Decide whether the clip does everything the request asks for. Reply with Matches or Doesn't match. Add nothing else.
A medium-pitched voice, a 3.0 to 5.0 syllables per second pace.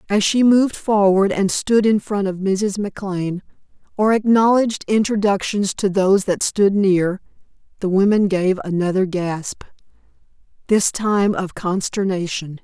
Doesn't match